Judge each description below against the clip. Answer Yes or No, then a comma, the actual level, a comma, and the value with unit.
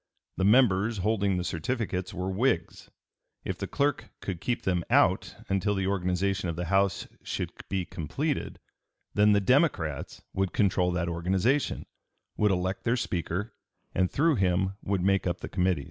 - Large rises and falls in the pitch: No, average, 2.8 semitones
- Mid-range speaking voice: No, very low, 95 Hz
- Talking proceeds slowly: No, average, 160 wpm